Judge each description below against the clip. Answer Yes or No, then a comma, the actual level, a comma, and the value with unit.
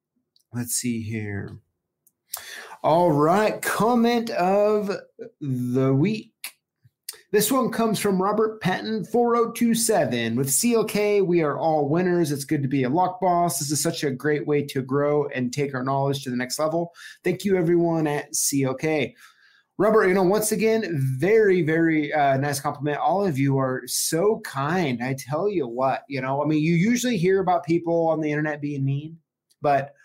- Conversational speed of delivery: Yes, average, 170 wpm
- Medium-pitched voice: Yes, medium, 160 Hz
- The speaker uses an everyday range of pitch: No, wide, 6.2 semitones